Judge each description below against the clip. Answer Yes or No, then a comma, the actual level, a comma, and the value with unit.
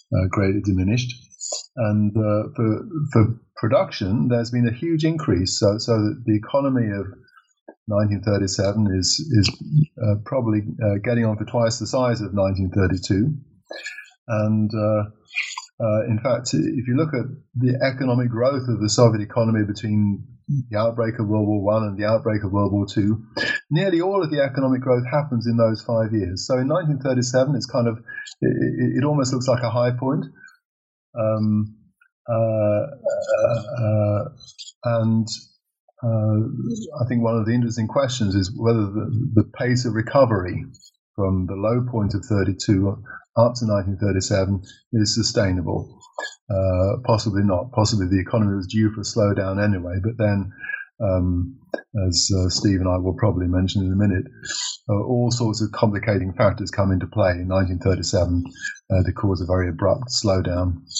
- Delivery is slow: No, average, 160 wpm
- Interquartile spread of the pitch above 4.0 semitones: No, average, 3.4 semitones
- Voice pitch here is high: No, low, 110 Hz